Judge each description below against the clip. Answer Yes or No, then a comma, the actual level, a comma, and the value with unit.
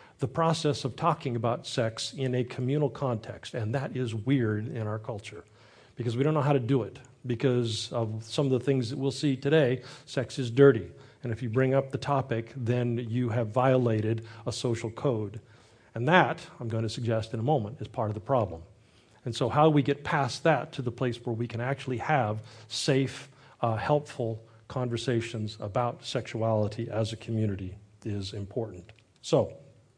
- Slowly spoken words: No, average, 185 wpm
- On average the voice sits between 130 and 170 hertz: No, low, 120 Hz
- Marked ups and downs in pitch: No, average, 3.4 semitones